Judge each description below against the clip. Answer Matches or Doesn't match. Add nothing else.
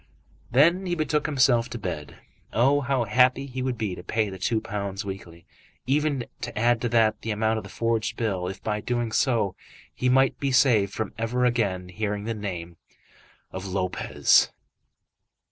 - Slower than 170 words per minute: Doesn't match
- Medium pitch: Doesn't match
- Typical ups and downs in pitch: Matches